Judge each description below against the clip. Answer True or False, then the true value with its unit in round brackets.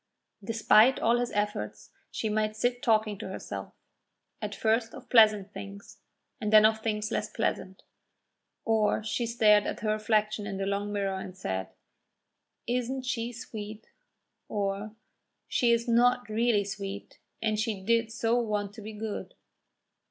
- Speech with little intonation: True (2.0 semitones)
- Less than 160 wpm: True (150 wpm)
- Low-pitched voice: False (215 Hz)